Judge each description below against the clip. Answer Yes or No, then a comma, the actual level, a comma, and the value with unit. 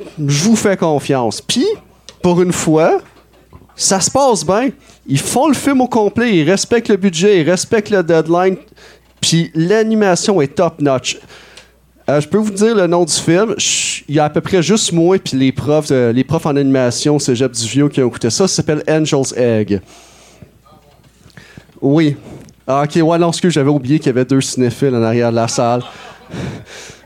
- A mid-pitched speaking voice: Yes, medium, 160 Hz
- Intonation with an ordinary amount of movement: No, wide, 5.7 semitones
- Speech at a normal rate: Yes, average, 185 wpm